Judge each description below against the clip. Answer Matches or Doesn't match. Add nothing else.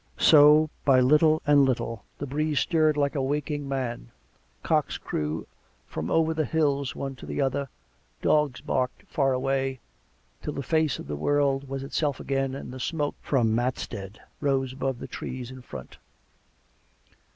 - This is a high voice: Doesn't match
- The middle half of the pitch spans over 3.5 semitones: Doesn't match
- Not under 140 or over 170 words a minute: Matches